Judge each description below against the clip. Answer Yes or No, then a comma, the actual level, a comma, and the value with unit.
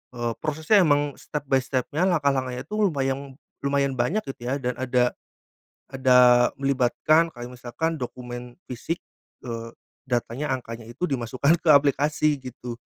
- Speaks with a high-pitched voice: No, low, 135 Hz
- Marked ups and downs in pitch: No, average, 3.2 semitones